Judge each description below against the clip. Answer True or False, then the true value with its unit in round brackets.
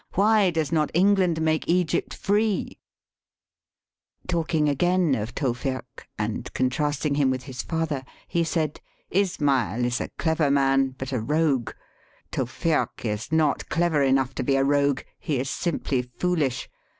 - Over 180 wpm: False (145 wpm)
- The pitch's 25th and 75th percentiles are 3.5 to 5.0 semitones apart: True (4.0 semitones)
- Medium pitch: True (145 Hz)